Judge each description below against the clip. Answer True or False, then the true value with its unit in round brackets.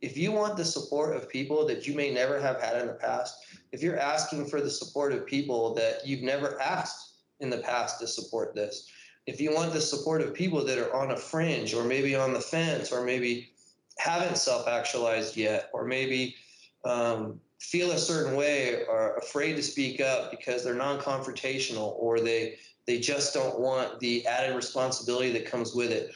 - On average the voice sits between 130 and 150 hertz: True (135 Hz)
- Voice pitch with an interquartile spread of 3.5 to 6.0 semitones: True (3.9 semitones)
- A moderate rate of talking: True (195 wpm)